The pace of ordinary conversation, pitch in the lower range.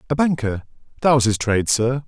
Yes: average, 175 wpm; low, 125 Hz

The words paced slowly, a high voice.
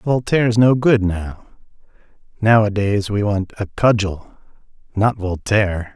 No: slow, 110 wpm; low, 105 Hz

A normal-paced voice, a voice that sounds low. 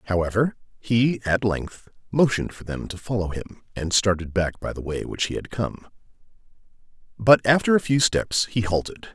Yes: average, 175 wpm; low, 110 Hz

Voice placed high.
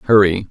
No: low, 100 Hz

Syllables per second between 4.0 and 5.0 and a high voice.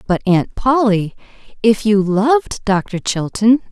No: 3.8 syllables/s; high, 215 Hz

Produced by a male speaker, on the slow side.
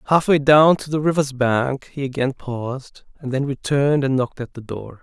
No: male; fast, 205 wpm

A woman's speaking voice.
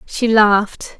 Yes: female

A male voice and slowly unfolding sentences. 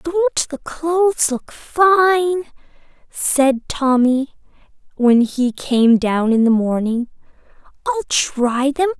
No: female; slow, 120 wpm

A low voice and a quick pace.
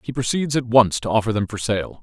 Yes: low, 115 Hz; fast, 265 wpm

